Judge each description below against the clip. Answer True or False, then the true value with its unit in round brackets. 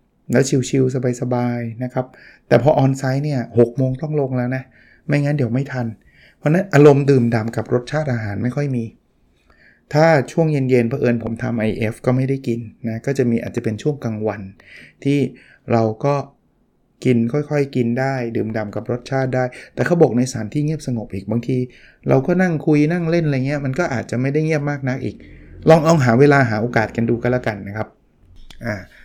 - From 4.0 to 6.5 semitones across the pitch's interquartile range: False (3.5 semitones)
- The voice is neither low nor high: False (125 Hz)